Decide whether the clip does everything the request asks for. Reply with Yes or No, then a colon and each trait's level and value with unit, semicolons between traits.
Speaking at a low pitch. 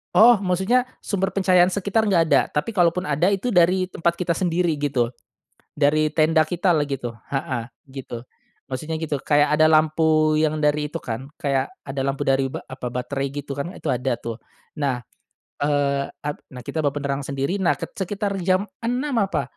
No: medium, 155 Hz